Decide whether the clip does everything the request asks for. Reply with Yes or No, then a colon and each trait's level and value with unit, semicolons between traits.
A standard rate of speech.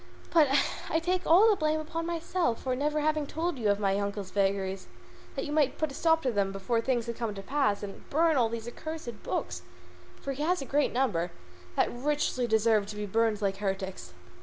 No: fast, 220 wpm